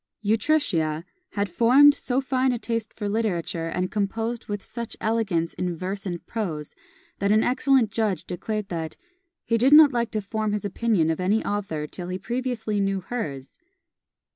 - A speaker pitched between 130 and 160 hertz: No, high, 210 Hz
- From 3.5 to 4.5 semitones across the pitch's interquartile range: Yes, average, 4.2 semitones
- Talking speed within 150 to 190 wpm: Yes, average, 165 wpm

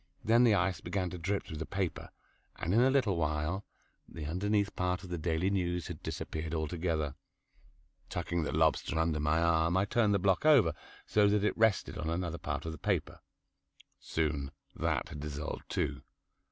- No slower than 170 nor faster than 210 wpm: Yes, average, 180 wpm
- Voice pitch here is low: Yes, very low, 85 Hz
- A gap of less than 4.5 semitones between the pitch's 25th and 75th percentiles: Yes, average, 3.8 semitones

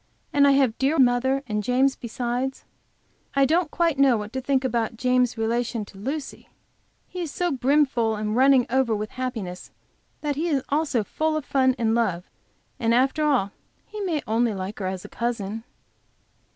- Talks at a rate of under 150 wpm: No, average, 180 wpm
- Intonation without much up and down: No, average, 3.7 semitones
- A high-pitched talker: Yes, very high, 255 Hz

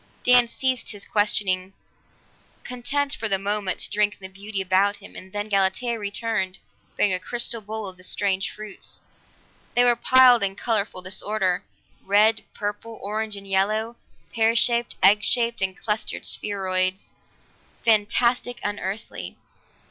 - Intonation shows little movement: No, average, 3.0 semitones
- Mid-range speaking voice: No, high, 210 Hz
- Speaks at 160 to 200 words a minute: No, average, 140 wpm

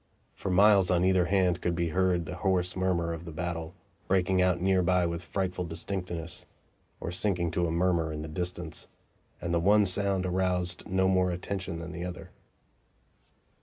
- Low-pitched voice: Yes, very low, 90 Hz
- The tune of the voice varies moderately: No, narrow, 1.5 semitones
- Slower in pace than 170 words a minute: No, average, 175 wpm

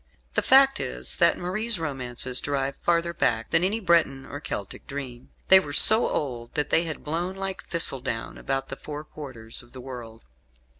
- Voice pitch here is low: No, medium, 145 Hz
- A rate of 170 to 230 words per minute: Yes, average, 180 wpm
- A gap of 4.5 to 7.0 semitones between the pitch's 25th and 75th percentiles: Yes, average, 5.2 semitones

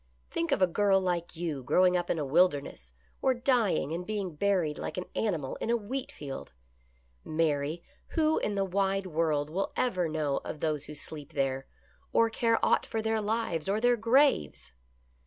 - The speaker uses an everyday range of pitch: No, wide, 6.0 semitones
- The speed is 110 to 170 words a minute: No, average, 180 wpm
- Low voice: No, medium, 180 Hz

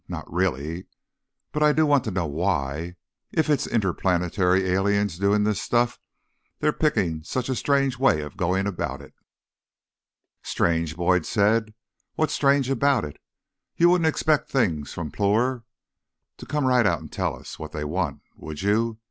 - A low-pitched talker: Yes, low, 100 Hz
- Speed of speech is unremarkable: Yes, average, 160 wpm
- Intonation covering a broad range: Yes, wide, 7.1 semitones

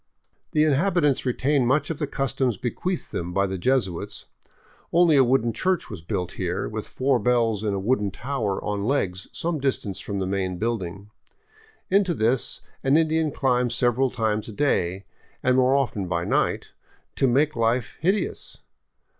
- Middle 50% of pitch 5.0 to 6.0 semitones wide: Yes, wide, 5.6 semitones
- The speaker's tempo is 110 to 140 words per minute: No, average, 165 wpm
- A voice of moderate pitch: No, low, 125 Hz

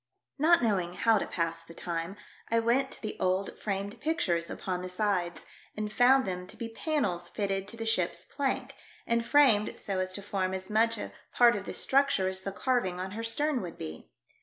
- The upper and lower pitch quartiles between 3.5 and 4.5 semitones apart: Yes, average, 4.1 semitones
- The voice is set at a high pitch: Yes, high, 200 Hz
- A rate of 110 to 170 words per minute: No, fast, 205 wpm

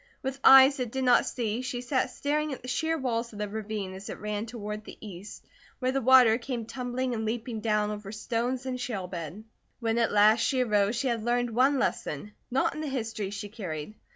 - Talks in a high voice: Yes, high, 230 Hz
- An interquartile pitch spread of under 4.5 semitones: Yes, average, 3.4 semitones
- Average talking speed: No, fast, 215 wpm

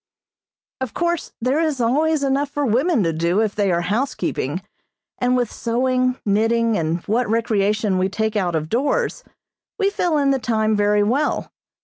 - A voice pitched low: No, high, 230 Hz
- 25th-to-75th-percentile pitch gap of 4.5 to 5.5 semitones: Yes, average, 4.9 semitones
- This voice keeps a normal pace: Yes, average, 165 wpm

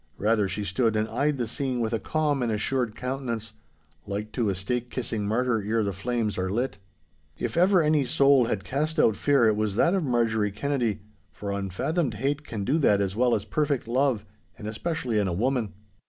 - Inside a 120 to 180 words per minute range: No, average, 200 wpm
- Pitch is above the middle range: No, low, 115 Hz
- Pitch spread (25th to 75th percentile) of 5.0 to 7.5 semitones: No, average, 4.5 semitones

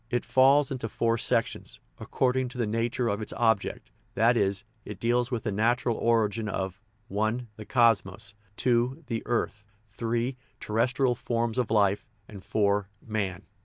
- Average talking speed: Yes, average, 155 wpm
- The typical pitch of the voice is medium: No, low, 115 Hz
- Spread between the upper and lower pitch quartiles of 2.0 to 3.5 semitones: Yes, average, 2.8 semitones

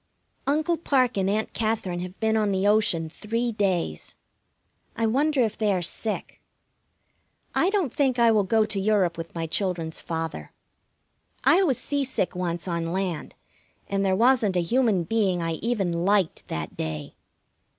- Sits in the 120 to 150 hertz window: No, high, 200 Hz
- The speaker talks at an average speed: Yes, average, 160 wpm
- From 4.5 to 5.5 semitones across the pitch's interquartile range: Yes, average, 4.8 semitones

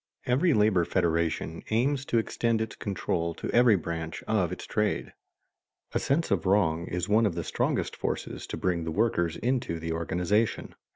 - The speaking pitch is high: No, very low, 95 Hz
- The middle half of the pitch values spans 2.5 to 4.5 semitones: No, average, 5.2 semitones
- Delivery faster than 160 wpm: Yes, average, 175 wpm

